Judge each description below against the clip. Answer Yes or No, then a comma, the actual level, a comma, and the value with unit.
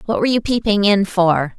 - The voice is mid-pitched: No, high, 200 Hz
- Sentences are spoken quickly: Yes, fast, 230 wpm